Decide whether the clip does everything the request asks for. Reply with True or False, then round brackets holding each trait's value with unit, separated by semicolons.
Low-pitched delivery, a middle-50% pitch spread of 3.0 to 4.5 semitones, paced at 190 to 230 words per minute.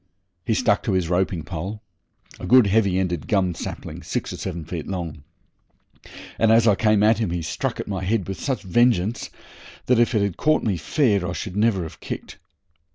True (95 Hz; 4.1 semitones; 200 wpm)